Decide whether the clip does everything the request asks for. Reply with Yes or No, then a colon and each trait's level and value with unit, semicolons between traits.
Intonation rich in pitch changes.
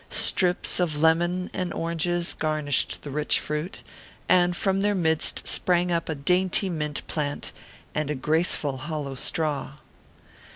No: average, 2.9 semitones